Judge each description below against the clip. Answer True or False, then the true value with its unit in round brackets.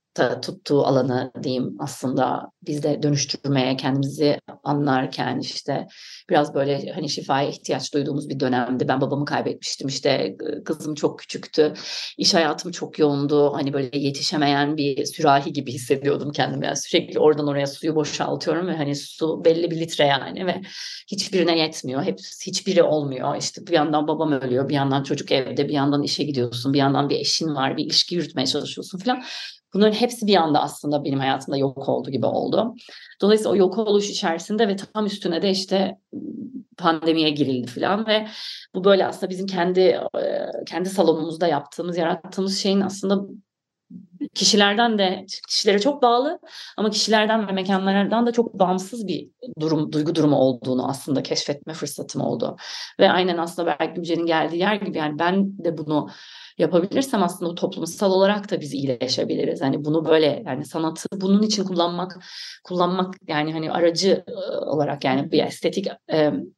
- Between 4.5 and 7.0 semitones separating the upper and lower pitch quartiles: True (5.2 semitones)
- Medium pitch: True (165 Hz)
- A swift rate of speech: True (155 wpm)